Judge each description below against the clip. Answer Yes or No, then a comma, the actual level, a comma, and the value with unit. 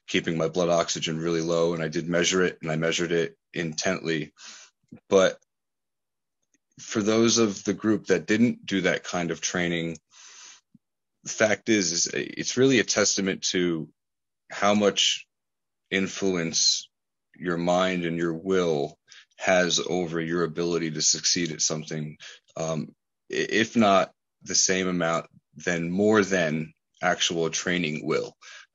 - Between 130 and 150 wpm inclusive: Yes, average, 140 wpm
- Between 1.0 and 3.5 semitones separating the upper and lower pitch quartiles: Yes, narrow, 2.5 semitones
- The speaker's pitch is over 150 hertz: No, very low, 85 Hz